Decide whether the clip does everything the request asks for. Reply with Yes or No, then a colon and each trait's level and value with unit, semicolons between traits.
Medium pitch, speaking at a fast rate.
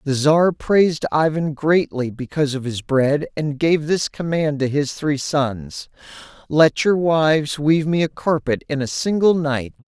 No: medium, 150 Hz; average, 170 wpm